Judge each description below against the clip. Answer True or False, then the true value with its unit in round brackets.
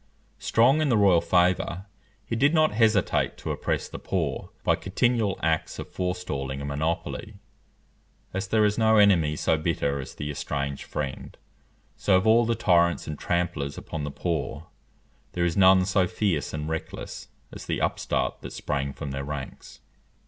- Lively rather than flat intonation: True (5.7 semitones)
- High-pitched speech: False (90 Hz)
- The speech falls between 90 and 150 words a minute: False (165 wpm)